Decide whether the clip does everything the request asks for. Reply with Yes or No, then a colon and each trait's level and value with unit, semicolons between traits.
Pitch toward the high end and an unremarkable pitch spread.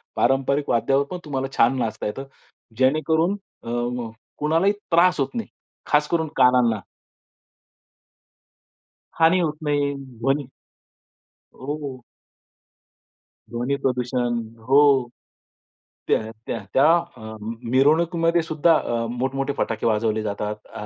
No: low, 135 Hz; average, 4.2 semitones